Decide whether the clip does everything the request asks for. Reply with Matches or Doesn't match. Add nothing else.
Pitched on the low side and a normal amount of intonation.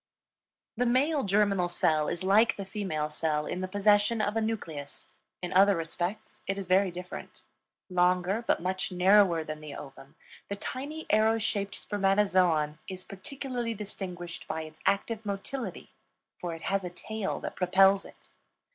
Doesn't match